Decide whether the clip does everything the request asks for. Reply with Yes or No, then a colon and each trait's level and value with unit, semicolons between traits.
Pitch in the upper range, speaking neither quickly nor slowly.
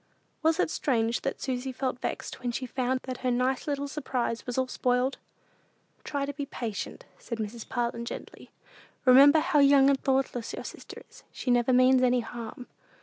Yes: very high, 255 Hz; average, 180 wpm